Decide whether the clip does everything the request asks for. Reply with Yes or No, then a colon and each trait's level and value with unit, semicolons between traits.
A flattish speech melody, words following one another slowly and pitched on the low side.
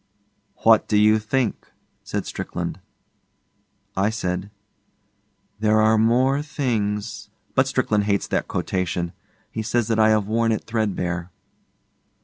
Yes: narrow, 2.0 semitones; slow, 130 wpm; low, 110 Hz